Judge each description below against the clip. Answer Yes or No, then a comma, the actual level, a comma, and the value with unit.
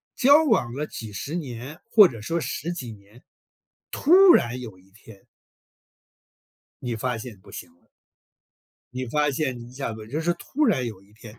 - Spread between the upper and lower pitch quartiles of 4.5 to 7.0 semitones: Yes, wide, 5.5 semitones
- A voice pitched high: No, low, 125 Hz